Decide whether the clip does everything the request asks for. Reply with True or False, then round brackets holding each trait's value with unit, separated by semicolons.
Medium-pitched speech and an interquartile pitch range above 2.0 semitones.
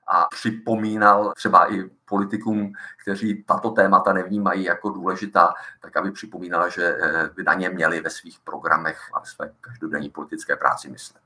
False (105 Hz; 2.7 semitones)